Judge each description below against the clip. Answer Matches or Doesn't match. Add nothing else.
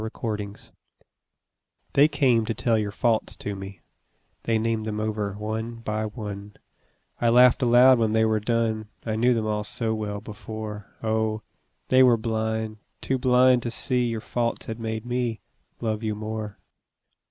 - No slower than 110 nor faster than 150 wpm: Doesn't match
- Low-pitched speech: Matches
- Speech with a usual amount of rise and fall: Doesn't match